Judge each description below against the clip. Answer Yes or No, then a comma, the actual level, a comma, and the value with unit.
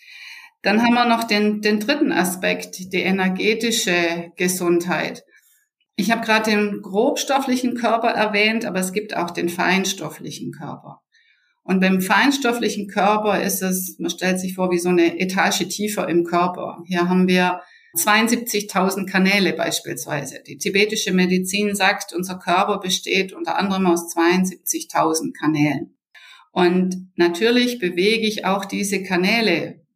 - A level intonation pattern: No, average, 3.2 semitones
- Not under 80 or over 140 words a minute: Yes, average, 135 wpm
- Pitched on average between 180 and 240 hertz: Yes, high, 190 Hz